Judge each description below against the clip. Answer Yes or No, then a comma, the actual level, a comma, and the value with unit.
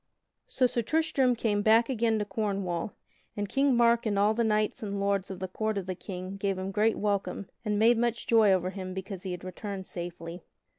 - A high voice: Yes, high, 205 Hz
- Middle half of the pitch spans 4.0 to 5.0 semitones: No, average, 3.0 semitones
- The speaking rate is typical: No, fast, 215 wpm